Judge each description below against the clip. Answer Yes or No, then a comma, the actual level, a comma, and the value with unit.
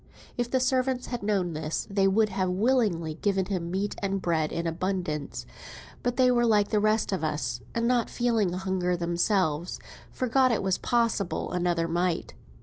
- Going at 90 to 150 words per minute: No, average, 170 wpm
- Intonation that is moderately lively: Yes, average, 5.0 semitones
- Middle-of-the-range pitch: No, high, 195 Hz